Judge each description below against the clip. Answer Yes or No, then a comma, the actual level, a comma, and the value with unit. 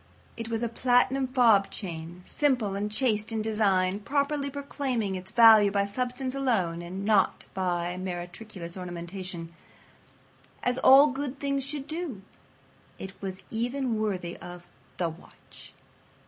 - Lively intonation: Yes, wide, 5.7 semitones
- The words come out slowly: Yes, slow, 130 wpm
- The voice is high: Yes, high, 215 Hz